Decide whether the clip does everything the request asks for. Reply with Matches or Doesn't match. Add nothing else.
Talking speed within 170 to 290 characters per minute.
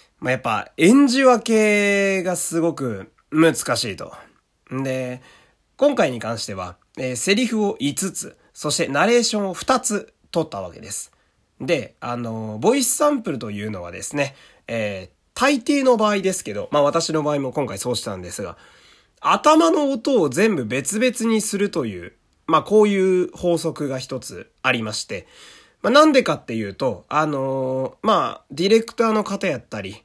Matches